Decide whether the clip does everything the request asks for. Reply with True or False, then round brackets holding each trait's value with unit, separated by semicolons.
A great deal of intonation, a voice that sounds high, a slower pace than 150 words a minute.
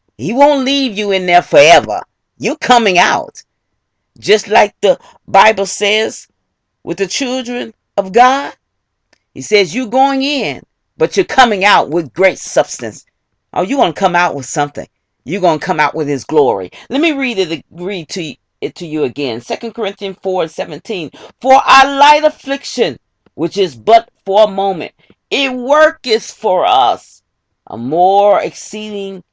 False (6.5 semitones; 205 Hz; 160 wpm)